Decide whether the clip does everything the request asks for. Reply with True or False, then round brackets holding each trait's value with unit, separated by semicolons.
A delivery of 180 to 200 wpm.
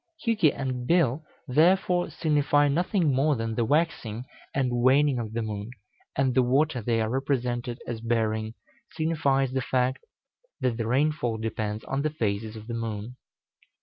False (155 wpm)